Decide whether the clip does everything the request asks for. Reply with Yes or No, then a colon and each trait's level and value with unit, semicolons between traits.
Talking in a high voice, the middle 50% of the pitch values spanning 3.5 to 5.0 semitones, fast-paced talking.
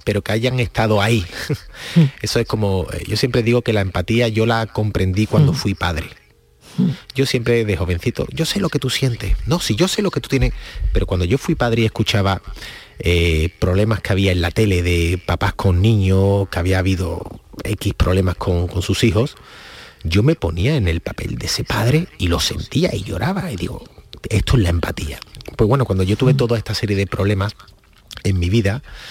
No: low, 105 Hz; average, 4.1 semitones; fast, 200 wpm